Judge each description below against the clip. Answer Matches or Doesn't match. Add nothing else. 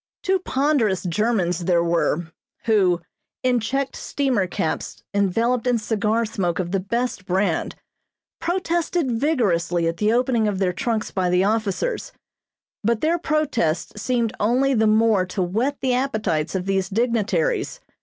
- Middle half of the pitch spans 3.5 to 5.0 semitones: Doesn't match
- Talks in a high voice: Matches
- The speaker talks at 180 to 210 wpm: Doesn't match